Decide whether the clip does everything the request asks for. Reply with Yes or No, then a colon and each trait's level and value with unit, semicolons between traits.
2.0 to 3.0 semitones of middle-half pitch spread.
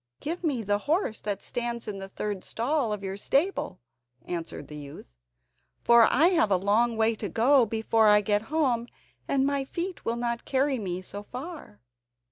No: average, 4.9 semitones